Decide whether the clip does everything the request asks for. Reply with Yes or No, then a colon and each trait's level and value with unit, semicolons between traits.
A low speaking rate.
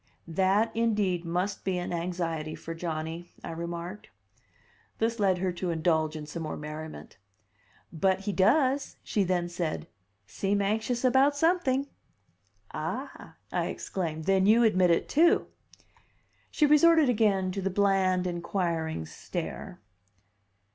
Yes: slow, 130 wpm